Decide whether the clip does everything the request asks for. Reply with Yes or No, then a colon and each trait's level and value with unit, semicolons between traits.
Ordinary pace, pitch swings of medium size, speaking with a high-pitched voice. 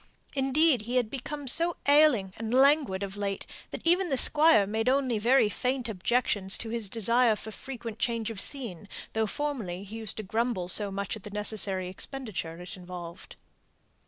Yes: average, 175 wpm; average, 4.9 semitones; high, 225 Hz